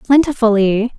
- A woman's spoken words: Yes, female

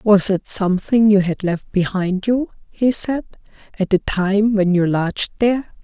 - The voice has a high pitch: Yes, high, 200 Hz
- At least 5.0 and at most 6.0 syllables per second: No, 4.5 syllables/s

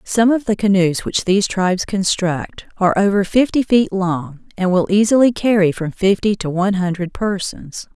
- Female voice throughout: Yes, female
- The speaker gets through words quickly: No, average, 175 wpm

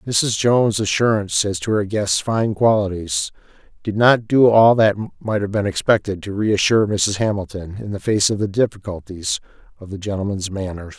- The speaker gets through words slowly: No, average, 175 wpm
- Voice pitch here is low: Yes, low, 105 Hz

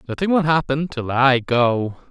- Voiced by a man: Yes, male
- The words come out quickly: No, average, 170 wpm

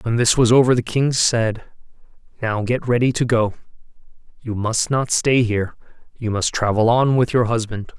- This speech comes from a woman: No, male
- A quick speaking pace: No, average, 165 wpm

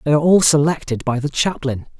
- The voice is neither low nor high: Yes, medium, 145 Hz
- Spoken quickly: Yes, fast, 210 wpm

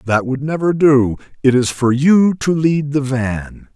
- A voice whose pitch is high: No, medium, 140 Hz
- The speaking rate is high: No, average, 190 wpm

